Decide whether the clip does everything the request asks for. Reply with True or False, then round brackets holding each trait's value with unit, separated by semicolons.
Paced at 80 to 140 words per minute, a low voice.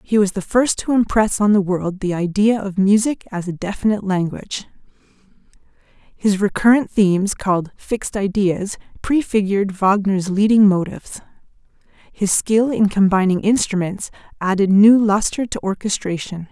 False (135 wpm; 200 Hz)